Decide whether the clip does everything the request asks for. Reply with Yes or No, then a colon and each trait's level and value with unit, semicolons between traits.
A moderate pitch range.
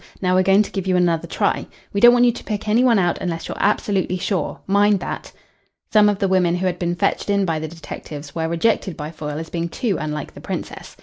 Yes: average, 3.6 semitones